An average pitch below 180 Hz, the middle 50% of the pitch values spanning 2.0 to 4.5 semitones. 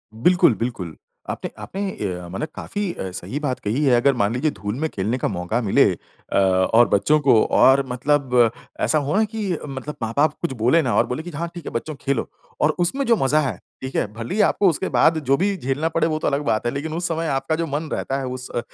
No: medium, 140 Hz; wide, 5.5 semitones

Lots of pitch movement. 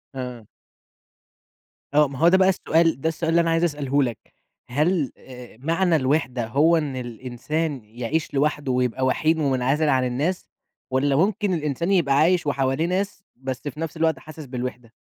No: average, 4.0 semitones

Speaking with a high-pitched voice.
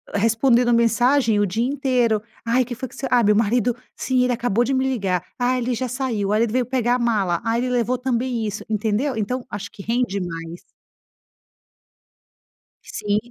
Yes: high, 235 Hz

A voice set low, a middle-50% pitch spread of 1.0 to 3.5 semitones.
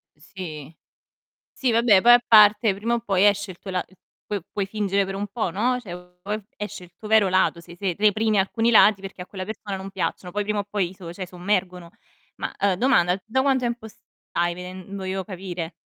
No: high, 195 Hz; narrow, 2.6 semitones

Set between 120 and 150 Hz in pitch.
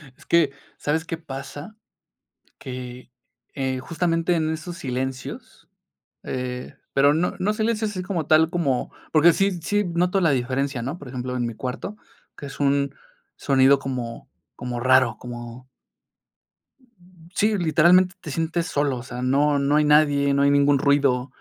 Yes: medium, 140 Hz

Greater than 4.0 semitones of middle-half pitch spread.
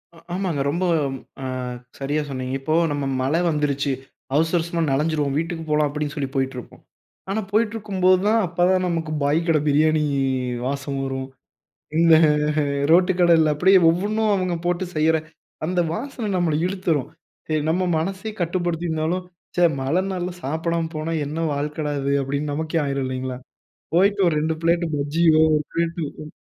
No: average, 3.4 semitones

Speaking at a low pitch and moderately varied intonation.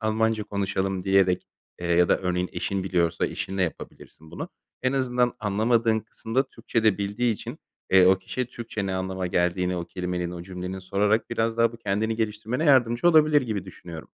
Yes: low, 100 Hz; average, 3.9 semitones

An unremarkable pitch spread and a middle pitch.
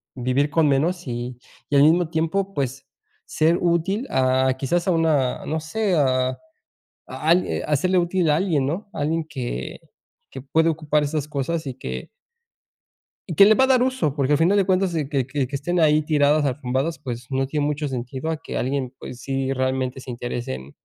Yes: average, 4.1 semitones; medium, 150 Hz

